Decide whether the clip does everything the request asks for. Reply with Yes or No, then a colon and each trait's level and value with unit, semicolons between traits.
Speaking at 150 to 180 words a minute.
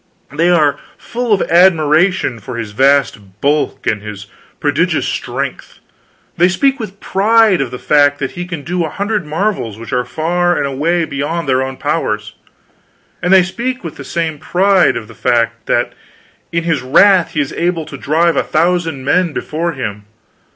Yes: average, 175 wpm